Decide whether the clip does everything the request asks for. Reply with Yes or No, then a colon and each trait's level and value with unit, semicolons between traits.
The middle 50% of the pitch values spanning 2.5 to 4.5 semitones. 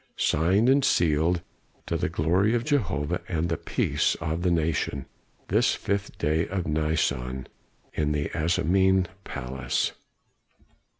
Yes: average, 4.0 semitones